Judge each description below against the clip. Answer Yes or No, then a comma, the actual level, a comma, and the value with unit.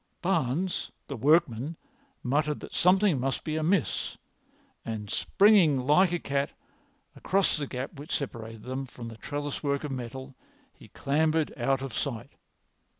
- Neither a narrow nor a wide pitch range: Yes, average, 3.9 semitones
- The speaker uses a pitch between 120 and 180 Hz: Yes, medium, 140 Hz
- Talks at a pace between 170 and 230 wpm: No, average, 145 wpm